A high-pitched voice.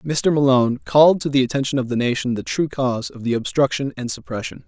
No: low, 135 Hz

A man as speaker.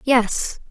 No: female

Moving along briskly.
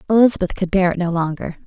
Yes: fast, 215 wpm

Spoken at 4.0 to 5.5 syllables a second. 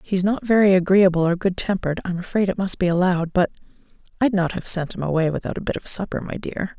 No: 6.4 syllables/s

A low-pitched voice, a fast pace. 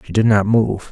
Yes: low, 105 Hz; fast, 260 wpm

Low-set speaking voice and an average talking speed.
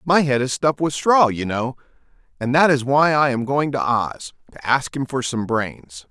No: low, 130 Hz; fast, 225 wpm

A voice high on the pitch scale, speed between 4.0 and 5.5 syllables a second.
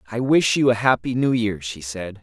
No: low, 115 Hz; 5.0 syllables/s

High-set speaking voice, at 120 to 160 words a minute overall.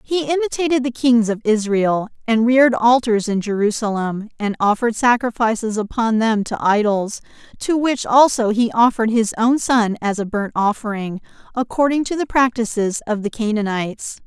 Yes: high, 230 Hz; average, 155 wpm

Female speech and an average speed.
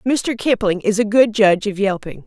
No: female; fast, 210 wpm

